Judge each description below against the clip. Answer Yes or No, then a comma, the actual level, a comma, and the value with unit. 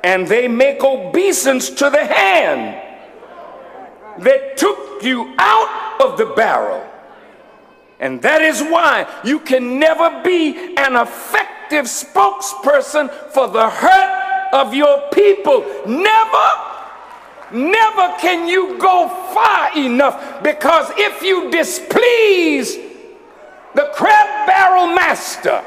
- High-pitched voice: Yes, very high, 325 Hz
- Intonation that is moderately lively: No, wide, 6.0 semitones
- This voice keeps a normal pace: No, slow, 110 wpm